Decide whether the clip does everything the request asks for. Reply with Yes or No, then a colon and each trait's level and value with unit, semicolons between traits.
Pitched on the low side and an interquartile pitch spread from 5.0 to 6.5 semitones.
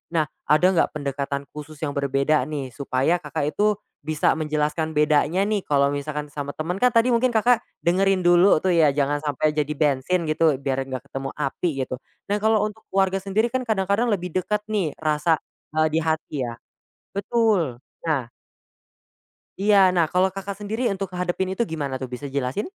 No: medium, 160 Hz; average, 5.3 semitones